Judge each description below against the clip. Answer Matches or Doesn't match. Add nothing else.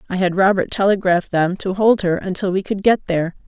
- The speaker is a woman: Matches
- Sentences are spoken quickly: Matches